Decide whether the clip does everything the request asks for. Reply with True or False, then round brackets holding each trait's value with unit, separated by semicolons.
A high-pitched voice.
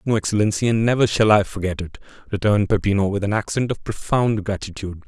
False (105 Hz)